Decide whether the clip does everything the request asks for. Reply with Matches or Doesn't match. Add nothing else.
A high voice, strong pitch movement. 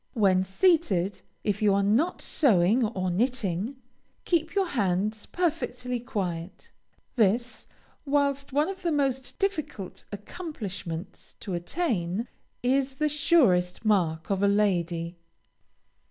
Matches